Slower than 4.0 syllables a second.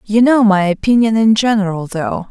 No: 5.0 syllables/s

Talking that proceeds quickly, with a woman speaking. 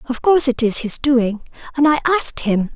No: average, 195 wpm; female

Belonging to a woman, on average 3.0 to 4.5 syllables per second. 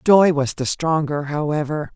Yes: female; 4.2 syllables/s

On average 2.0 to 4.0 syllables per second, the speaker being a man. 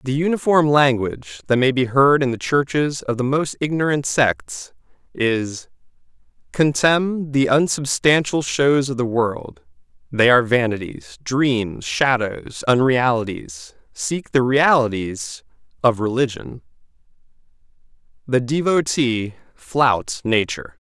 Yes: 3.9 syllables/s; male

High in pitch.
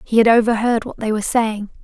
Yes: high, 225 Hz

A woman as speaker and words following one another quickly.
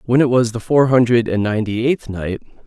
No: male; fast, 225 wpm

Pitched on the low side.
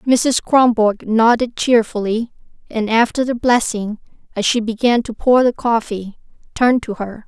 No: high, 230 Hz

